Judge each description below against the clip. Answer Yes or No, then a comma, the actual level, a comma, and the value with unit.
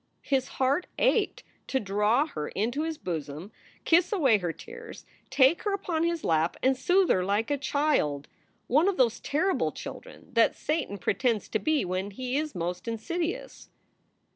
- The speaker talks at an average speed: Yes, average, 165 wpm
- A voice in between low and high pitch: No, very high, 260 Hz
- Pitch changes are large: Yes, wide, 8.1 semitones